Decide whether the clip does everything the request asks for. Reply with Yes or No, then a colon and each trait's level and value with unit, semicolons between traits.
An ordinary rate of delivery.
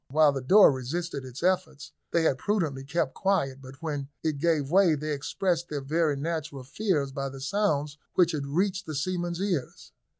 Yes: average, 180 wpm